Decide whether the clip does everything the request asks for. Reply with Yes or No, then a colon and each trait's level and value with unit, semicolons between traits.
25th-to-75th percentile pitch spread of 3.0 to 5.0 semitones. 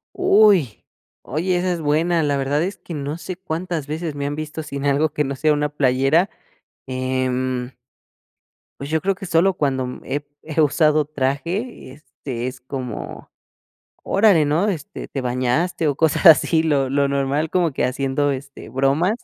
Yes: average, 3.5 semitones